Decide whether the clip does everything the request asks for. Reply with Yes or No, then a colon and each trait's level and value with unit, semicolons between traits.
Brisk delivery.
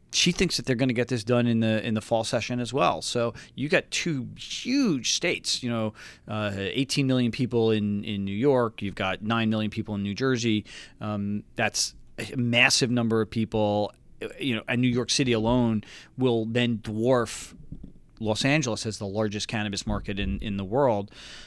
No: average, 195 wpm